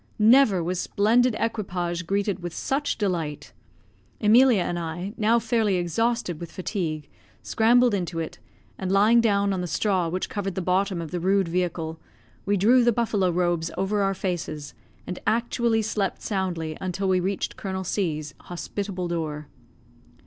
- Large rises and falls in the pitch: No, average, 3.5 semitones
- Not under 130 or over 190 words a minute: Yes, average, 155 wpm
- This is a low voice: No, high, 190 Hz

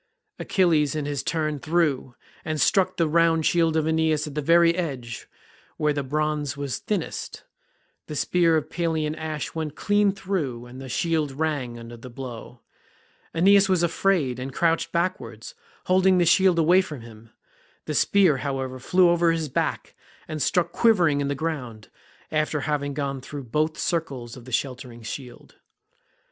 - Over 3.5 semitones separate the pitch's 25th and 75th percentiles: Yes, average, 3.9 semitones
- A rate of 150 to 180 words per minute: Yes, average, 160 wpm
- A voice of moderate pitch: Yes, medium, 155 Hz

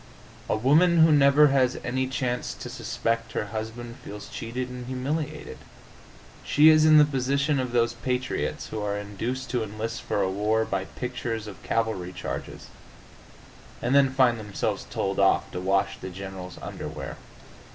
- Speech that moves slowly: No, average, 160 wpm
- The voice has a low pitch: Yes, low, 120 Hz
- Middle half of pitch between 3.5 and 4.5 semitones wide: Yes, average, 3.8 semitones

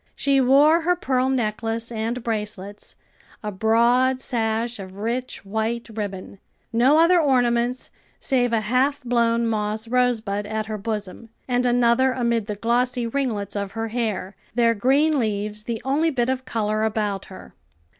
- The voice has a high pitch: Yes, high, 230 Hz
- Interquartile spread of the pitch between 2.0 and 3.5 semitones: Yes, average, 2.9 semitones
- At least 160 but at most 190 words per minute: No, average, 150 wpm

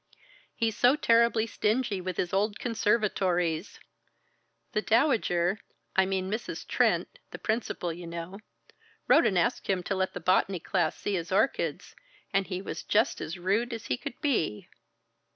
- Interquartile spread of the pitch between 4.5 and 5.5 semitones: No, average, 4.0 semitones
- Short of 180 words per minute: Yes, average, 155 wpm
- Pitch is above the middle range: Yes, high, 195 Hz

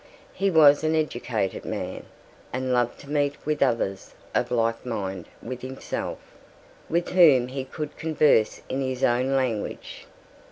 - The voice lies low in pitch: Yes, low, 130 Hz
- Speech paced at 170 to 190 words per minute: No, average, 145 wpm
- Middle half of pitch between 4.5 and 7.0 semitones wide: No, average, 3.8 semitones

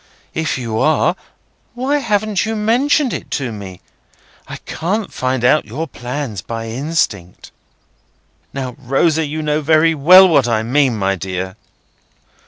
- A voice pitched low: No, medium, 145 Hz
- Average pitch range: No, wide, 6.3 semitones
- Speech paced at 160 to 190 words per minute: No, average, 140 wpm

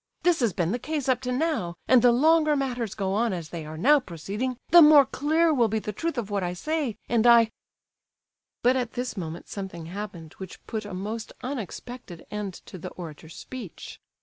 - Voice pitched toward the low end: No, high, 230 Hz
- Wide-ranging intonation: Yes, wide, 5.7 semitones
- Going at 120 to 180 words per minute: No, average, 200 wpm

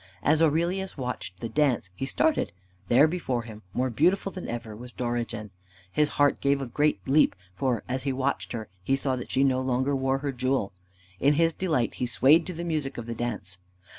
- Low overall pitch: Yes, low, 130 Hz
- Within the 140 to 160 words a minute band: No, average, 200 wpm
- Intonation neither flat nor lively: Yes, average, 3.9 semitones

